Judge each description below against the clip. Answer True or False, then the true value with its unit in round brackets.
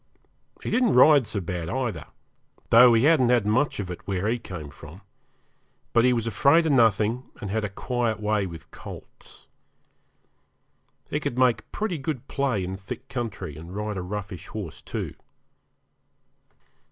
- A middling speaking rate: True (160 wpm)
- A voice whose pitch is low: True (110 Hz)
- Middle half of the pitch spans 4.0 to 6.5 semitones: True (4.7 semitones)